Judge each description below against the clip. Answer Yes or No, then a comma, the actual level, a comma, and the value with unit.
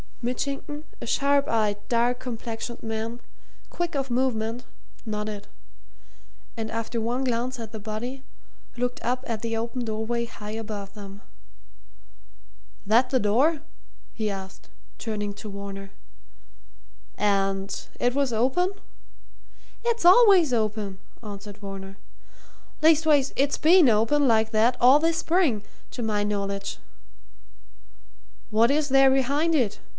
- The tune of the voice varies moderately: Yes, average, 4.2 semitones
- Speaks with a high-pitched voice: Yes, high, 230 Hz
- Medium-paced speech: No, slow, 125 wpm